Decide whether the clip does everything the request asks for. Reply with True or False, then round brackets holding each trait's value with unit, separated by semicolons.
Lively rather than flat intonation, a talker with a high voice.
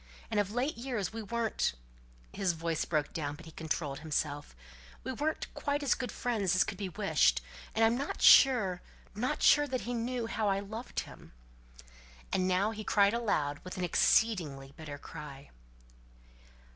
True (6.5 semitones; 200 Hz)